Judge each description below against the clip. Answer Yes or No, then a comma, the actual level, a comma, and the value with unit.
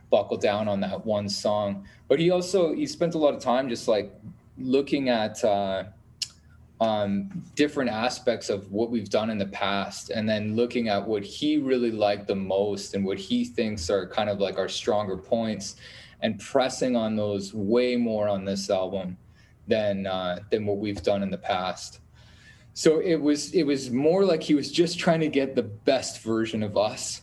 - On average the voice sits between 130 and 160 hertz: No, low, 110 Hz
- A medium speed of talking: Yes, average, 190 wpm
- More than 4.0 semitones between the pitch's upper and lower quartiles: Yes, average, 4.4 semitones